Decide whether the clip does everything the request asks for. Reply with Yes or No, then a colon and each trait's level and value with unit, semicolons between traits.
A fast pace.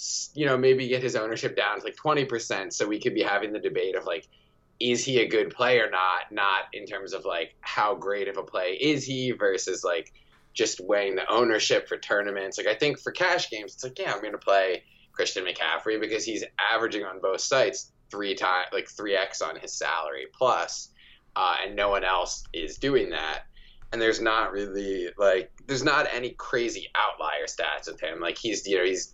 Yes: fast, 210 wpm